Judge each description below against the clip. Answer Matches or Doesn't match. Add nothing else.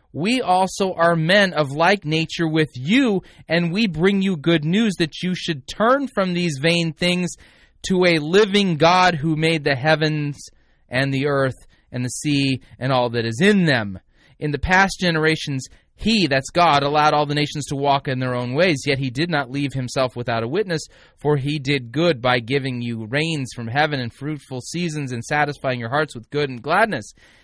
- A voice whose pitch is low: Doesn't match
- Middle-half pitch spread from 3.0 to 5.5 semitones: Matches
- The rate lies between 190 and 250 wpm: Matches